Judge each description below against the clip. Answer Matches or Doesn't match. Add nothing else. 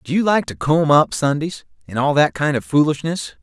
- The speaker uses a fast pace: Matches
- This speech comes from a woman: Doesn't match